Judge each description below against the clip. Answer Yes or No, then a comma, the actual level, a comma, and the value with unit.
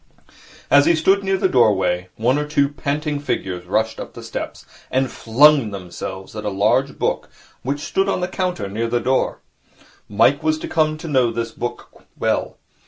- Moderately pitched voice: No, low, 130 Hz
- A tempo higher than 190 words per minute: No, average, 180 wpm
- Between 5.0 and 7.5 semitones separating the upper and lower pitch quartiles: Yes, wide, 5.6 semitones